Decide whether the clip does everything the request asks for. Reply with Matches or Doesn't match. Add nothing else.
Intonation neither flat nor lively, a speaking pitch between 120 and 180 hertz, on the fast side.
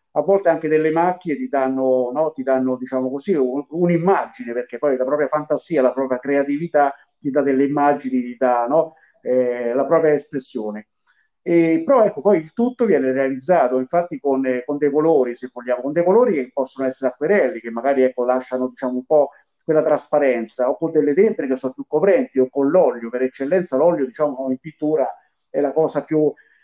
Matches